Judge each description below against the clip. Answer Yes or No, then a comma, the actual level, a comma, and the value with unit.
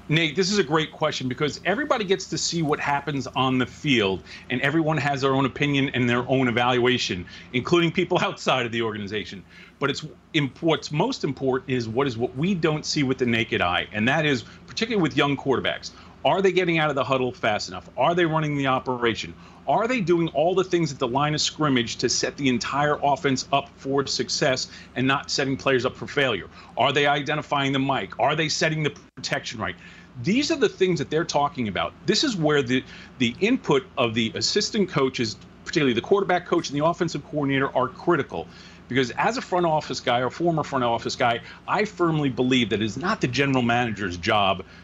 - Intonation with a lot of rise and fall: No, average, 4.6 semitones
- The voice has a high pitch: No, medium, 140 Hz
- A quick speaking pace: Yes, fast, 210 wpm